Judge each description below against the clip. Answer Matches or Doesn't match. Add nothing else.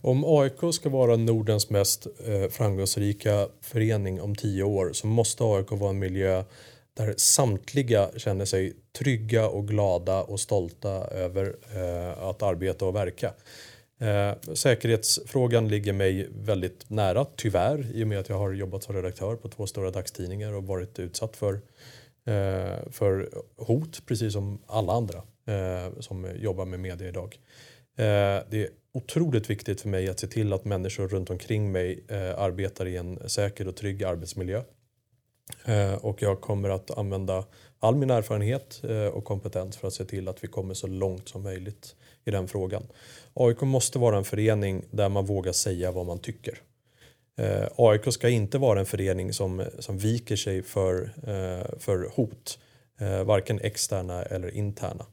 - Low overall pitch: Matches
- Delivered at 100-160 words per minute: Matches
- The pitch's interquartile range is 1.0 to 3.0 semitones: Doesn't match